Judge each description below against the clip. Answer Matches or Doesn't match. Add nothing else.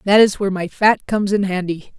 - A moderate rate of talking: Doesn't match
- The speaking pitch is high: Matches